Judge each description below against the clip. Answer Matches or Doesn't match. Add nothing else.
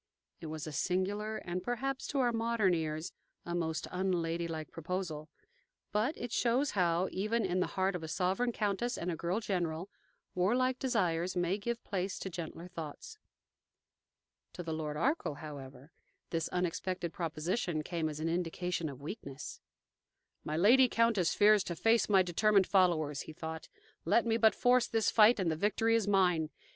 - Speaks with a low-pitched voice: Doesn't match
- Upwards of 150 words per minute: Matches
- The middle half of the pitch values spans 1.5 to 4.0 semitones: Doesn't match